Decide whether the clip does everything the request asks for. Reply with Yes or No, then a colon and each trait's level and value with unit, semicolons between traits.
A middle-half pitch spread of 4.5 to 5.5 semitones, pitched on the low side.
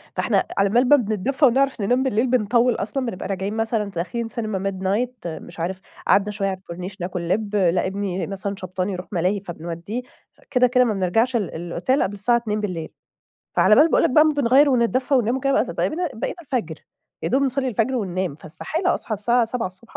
No: average, 4.9 semitones; high, 215 Hz